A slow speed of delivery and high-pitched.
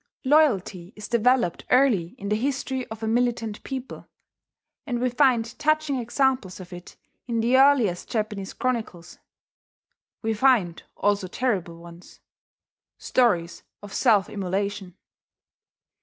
Yes: slow, 120 wpm; high, 225 Hz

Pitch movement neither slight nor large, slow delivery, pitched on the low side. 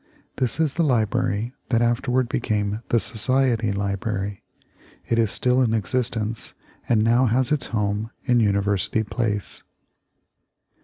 Yes: average, 3.2 semitones; slow, 125 wpm; low, 115 Hz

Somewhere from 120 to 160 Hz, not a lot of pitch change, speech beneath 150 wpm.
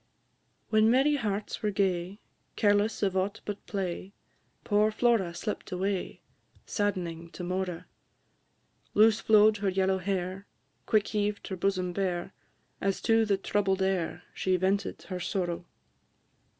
No: high, 195 Hz; narrow, 2.2 semitones; slow, 135 wpm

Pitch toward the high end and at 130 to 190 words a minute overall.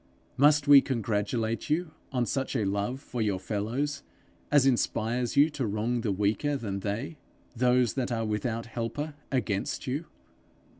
No: low, 120 Hz; average, 150 wpm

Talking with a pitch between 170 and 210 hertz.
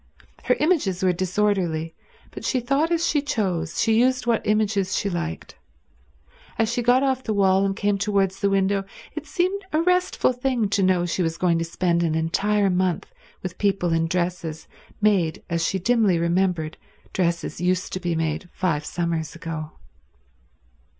Yes: high, 190 Hz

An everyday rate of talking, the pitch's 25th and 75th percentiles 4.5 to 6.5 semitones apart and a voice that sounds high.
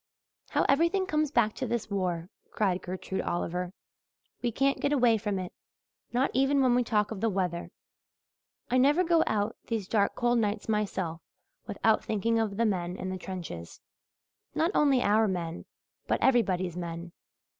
Yes: average, 165 wpm; average, 5.2 semitones; high, 215 Hz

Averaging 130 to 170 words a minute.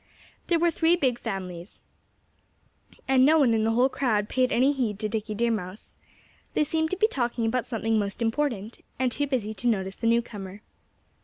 No: average, 185 wpm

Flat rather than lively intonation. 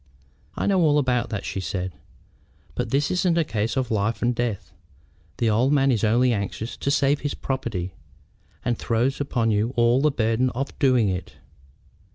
No: average, 3.9 semitones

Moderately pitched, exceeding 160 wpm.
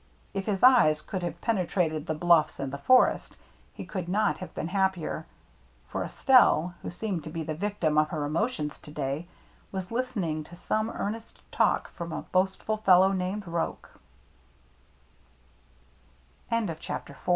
No: medium, 180 Hz; average, 145 wpm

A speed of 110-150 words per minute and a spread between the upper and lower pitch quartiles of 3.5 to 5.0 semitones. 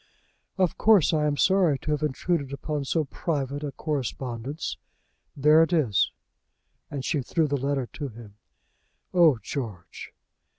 No: average, 140 wpm; average, 3.0 semitones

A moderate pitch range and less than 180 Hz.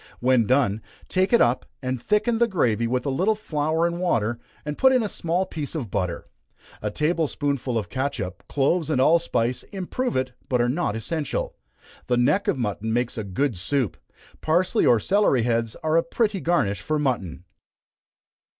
No: wide, 6.5 semitones; medium, 140 Hz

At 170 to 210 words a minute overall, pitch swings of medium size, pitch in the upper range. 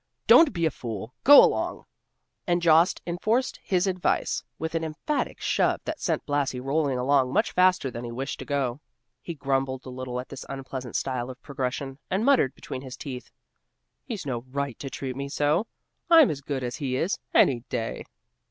No: average, 185 wpm; average, 5.0 semitones; medium, 140 Hz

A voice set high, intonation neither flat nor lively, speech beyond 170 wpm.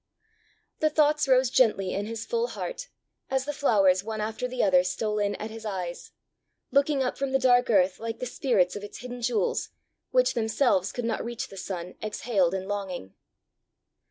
Yes: high, 225 Hz; average, 5.0 semitones; average, 185 wpm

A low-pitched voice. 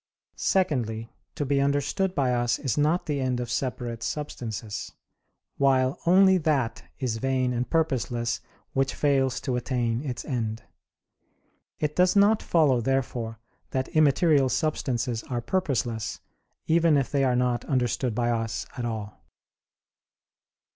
Yes: low, 130 Hz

